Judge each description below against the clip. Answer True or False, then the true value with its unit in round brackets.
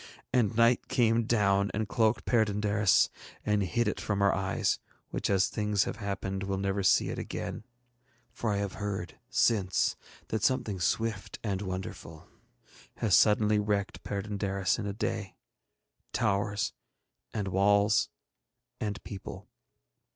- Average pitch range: False (1.8 semitones)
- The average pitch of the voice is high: False (100 Hz)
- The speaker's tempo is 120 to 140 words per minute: True (135 wpm)